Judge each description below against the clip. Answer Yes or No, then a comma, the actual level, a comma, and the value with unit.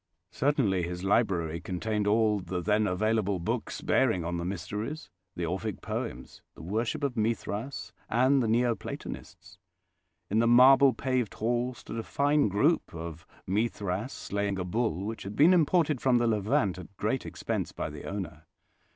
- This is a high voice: No, low, 105 Hz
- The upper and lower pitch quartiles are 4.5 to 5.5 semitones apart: Yes, average, 4.8 semitones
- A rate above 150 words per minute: Yes, average, 160 wpm